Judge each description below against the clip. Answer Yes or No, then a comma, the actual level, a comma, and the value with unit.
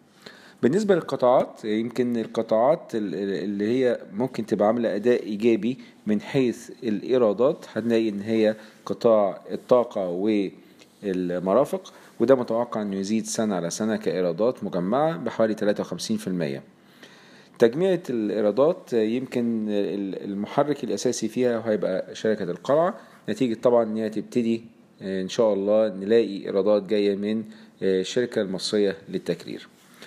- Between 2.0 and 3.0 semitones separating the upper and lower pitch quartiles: Yes, narrow, 2.6 semitones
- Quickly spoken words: No, average, 115 wpm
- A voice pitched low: Yes, low, 110 Hz